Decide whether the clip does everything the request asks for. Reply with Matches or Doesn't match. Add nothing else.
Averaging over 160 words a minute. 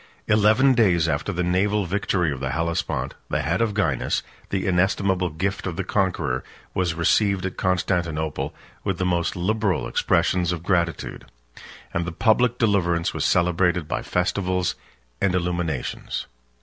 Doesn't match